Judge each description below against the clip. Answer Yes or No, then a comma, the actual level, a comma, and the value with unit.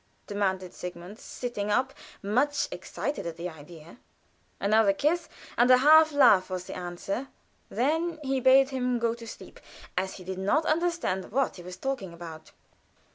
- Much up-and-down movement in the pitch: Yes, wide, 6.7 semitones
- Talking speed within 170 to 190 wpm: No, average, 160 wpm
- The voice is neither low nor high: No, high, 220 Hz